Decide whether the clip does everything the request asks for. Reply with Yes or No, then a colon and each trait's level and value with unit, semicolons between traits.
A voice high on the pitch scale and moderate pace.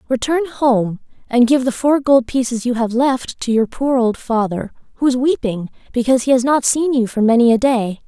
No: high, 245 Hz; fast, 215 wpm